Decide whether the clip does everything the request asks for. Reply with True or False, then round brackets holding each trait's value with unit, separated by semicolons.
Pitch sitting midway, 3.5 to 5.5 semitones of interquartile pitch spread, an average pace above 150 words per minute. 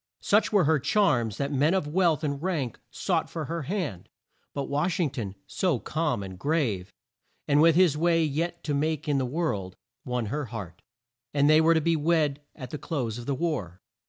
True (150 Hz; 4.6 semitones; 200 wpm)